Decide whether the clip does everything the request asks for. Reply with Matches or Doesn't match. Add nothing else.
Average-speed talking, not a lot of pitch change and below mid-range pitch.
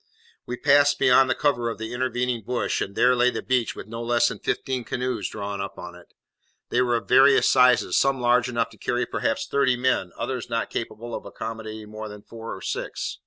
Doesn't match